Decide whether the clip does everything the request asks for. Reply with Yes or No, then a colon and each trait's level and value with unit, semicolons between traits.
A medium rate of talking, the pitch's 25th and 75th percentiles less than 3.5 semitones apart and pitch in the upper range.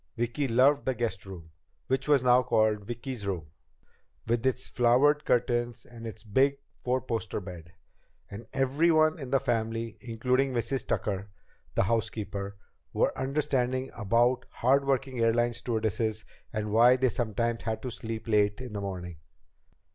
No: average, 145 wpm; average, 3.1 semitones; low, 120 Hz